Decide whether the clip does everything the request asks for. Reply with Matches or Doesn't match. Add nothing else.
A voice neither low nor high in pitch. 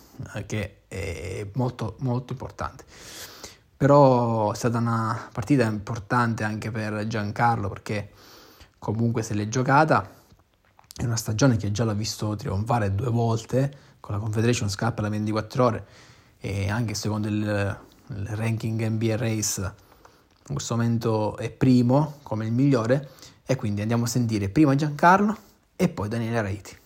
Doesn't match